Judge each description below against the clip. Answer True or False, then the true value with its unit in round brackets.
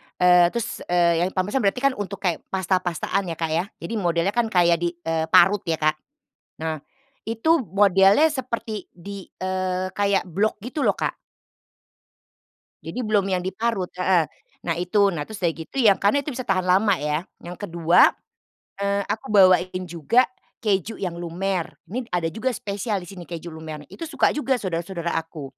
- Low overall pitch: False (185 Hz)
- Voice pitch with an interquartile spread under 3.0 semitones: False (3.3 semitones)